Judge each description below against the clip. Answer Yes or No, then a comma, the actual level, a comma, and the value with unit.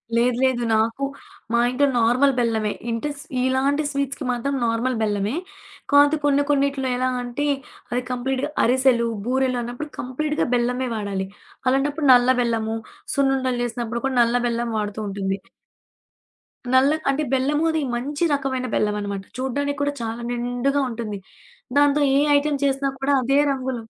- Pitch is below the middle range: No, very high, 255 Hz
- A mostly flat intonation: No, average, 3.0 semitones